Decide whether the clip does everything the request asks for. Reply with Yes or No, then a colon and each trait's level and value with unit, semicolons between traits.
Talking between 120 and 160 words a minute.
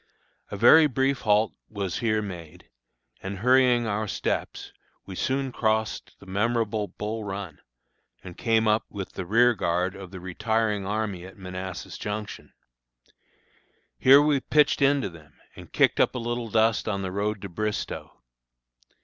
Yes: average, 150 wpm